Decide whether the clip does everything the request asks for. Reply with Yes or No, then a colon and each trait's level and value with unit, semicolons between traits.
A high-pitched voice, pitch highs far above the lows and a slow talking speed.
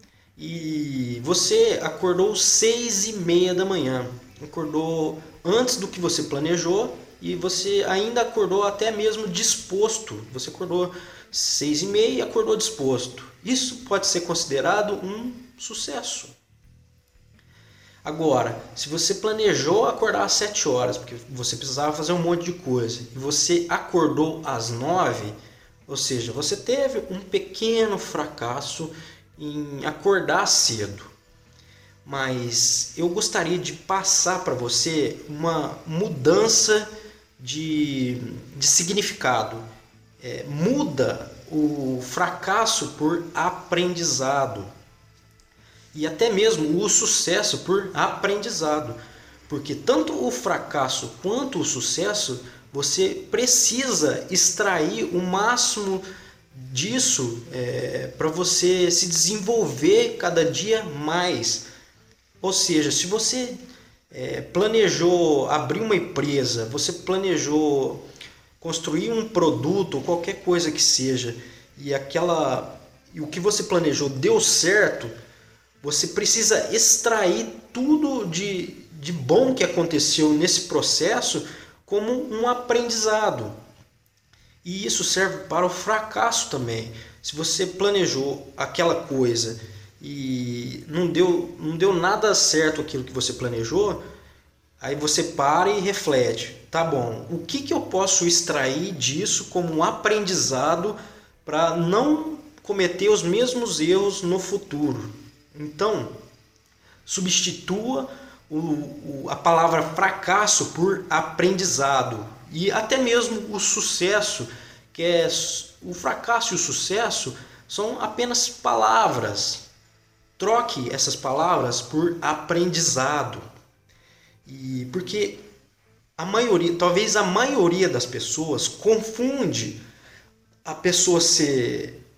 No: medium, 165 Hz; wide, 7.0 semitones; slow, 110 wpm